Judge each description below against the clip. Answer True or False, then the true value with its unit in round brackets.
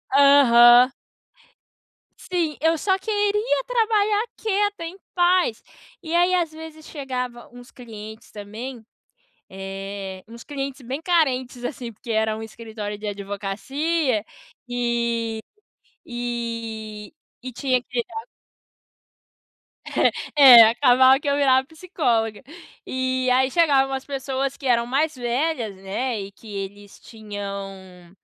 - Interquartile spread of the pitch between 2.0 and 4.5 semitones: False (5.4 semitones)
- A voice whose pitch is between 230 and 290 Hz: True (250 Hz)